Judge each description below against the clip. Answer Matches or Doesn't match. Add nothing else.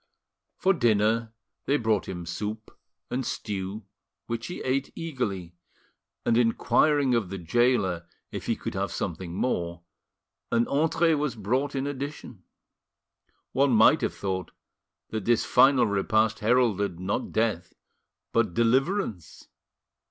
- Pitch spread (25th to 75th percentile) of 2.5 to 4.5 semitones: Doesn't match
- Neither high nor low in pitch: Doesn't match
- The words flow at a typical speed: Doesn't match